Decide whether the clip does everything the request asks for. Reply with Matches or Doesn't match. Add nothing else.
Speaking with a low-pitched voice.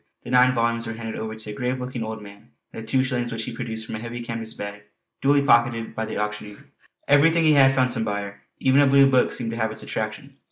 Matches